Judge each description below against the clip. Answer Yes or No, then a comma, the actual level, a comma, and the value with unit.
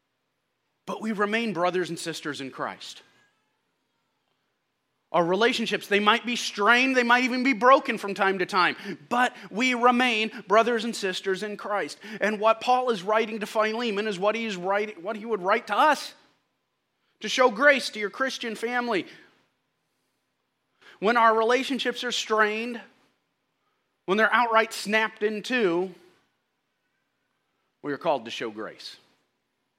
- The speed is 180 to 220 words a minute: No, average, 145 wpm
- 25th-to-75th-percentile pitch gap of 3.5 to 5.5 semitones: No, average, 3.1 semitones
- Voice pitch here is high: Yes, high, 225 Hz